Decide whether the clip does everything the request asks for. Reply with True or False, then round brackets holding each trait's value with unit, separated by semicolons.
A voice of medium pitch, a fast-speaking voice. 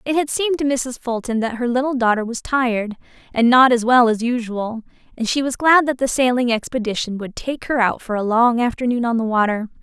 False (240 Hz; 225 wpm)